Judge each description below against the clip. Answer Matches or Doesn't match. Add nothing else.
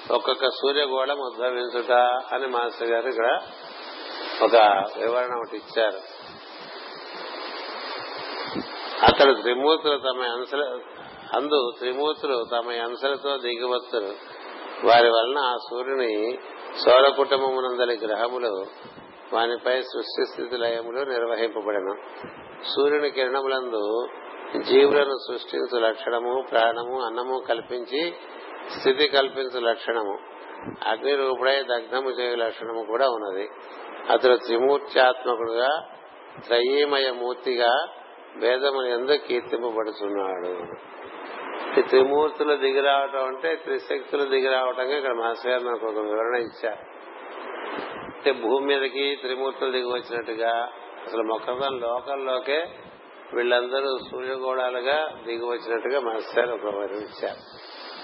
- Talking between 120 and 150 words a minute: Doesn't match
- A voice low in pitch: Matches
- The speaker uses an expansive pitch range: Doesn't match